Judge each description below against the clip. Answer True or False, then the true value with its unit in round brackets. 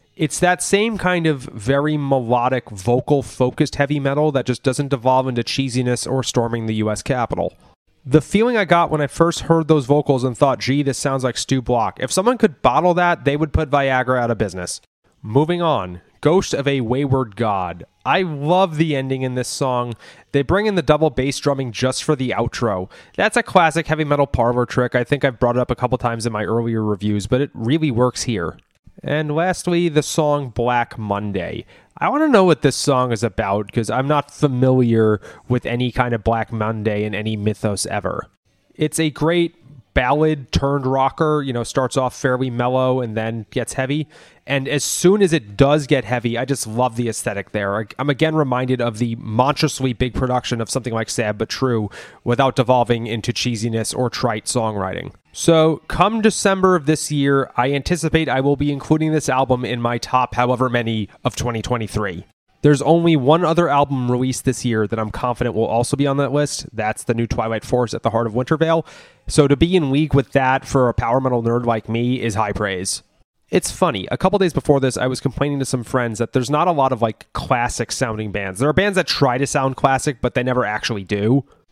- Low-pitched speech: True (130 Hz)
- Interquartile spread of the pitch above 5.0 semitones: False (3.8 semitones)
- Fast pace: True (210 wpm)